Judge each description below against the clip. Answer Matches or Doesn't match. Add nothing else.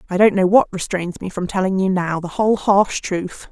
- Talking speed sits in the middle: Doesn't match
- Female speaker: Matches